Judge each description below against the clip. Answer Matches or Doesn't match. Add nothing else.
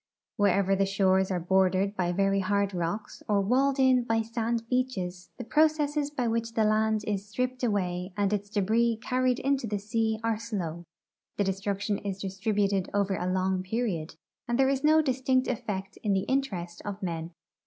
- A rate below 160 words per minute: Doesn't match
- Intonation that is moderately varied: Matches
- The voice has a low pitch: Doesn't match